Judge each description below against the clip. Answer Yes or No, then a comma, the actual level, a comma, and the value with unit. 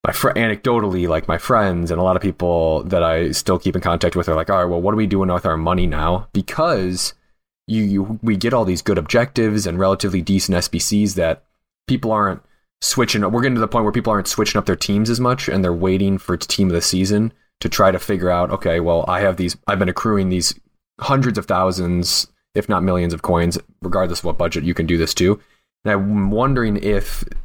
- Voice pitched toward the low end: Yes, very low, 95 Hz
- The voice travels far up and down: No, average, 3.2 semitones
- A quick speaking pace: Yes, fast, 235 wpm